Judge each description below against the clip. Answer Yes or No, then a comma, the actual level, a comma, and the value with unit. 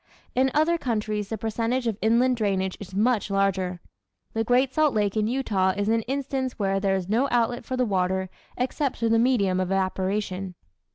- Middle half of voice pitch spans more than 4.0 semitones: Yes, average, 4.4 semitones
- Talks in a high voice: Yes, high, 220 Hz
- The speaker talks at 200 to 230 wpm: No, average, 185 wpm